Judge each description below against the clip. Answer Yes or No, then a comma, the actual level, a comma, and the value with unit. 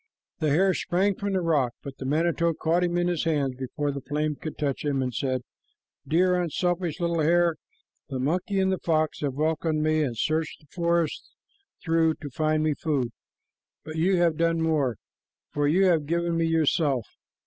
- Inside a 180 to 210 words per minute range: Yes, average, 185 wpm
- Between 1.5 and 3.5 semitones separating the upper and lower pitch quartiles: Yes, average, 2.8 semitones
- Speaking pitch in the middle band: Yes, medium, 160 Hz